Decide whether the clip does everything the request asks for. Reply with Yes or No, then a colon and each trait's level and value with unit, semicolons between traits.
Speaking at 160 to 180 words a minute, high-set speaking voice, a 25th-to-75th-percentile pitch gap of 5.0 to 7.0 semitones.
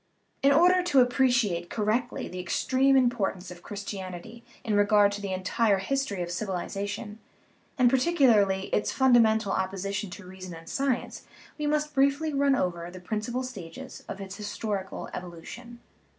No: average, 150 wpm; high, 210 Hz; average, 5.3 semitones